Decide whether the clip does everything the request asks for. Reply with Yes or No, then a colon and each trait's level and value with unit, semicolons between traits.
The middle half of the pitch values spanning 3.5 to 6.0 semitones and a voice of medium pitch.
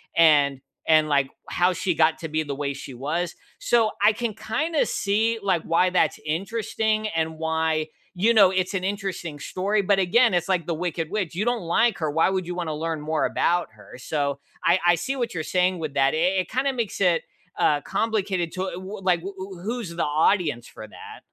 Yes: average, 4.2 semitones; medium, 175 Hz